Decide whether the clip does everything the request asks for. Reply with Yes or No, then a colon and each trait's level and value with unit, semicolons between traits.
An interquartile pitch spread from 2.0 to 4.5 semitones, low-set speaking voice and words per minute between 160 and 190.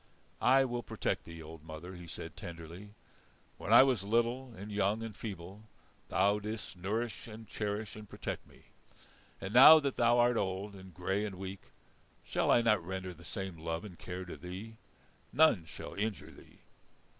Yes: average, 3.7 semitones; low, 100 Hz; average, 175 wpm